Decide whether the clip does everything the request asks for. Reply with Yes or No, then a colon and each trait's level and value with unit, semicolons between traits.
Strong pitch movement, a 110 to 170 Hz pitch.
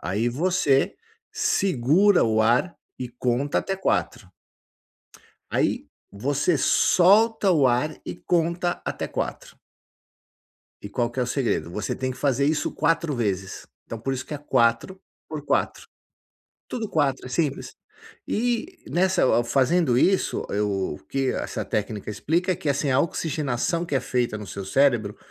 Yes: wide, 6.3 semitones; low, 135 Hz